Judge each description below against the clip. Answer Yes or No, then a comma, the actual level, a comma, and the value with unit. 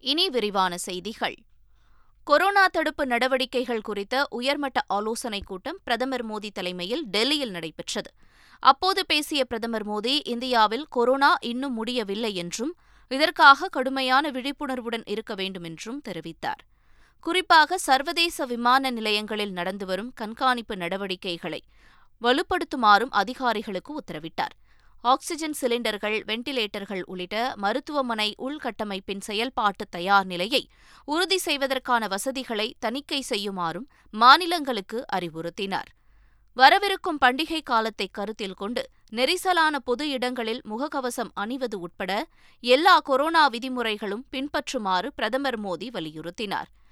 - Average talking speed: Yes, average, 95 wpm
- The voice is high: Yes, high, 240 Hz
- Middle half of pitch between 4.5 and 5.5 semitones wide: Yes, average, 5.1 semitones